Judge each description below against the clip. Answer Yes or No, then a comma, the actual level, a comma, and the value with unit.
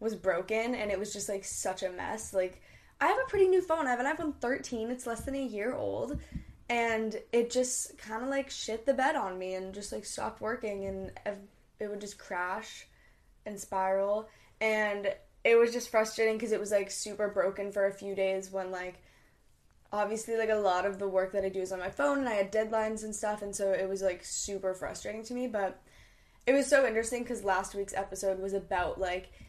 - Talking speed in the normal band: No, fast, 220 wpm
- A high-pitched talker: Yes, high, 210 Hz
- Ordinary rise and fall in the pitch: Yes, average, 3.3 semitones